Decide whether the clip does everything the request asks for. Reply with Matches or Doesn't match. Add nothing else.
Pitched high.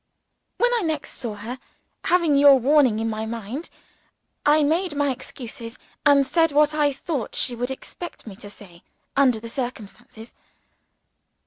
Matches